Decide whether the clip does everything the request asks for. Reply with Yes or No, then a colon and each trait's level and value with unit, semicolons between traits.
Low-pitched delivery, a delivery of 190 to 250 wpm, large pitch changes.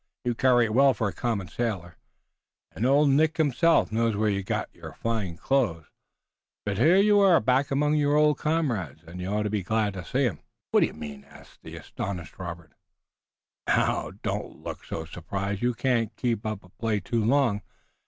Yes: low, 110 Hz; average, 195 wpm; wide, 6.0 semitones